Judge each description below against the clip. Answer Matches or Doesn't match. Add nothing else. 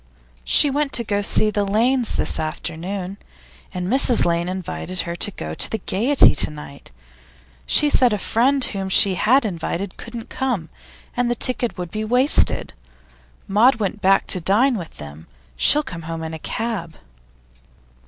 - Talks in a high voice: Matches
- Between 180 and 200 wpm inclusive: Doesn't match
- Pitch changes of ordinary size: Doesn't match